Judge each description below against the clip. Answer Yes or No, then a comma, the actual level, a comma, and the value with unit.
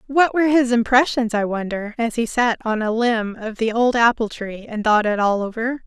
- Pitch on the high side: Yes, high, 230 Hz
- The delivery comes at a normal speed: No, fast, 225 wpm